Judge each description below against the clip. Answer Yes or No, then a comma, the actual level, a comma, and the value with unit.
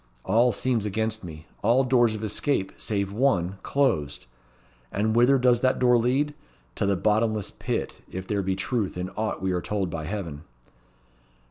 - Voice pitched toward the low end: Yes, low, 105 Hz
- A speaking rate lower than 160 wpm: No, average, 165 wpm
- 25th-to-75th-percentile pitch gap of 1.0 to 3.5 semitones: No, average, 4.4 semitones